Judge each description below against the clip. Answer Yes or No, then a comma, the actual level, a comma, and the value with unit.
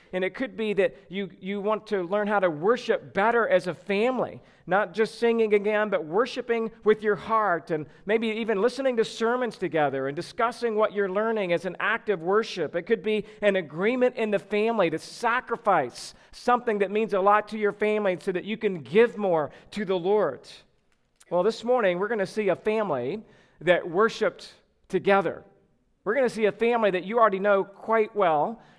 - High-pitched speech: Yes, high, 210 Hz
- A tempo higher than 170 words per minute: Yes, average, 195 wpm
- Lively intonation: No, average, 3.0 semitones